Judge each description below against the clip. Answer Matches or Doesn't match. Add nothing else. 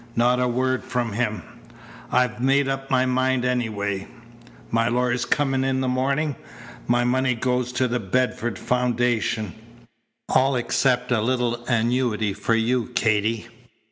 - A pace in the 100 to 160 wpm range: Matches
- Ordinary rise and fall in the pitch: Doesn't match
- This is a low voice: Matches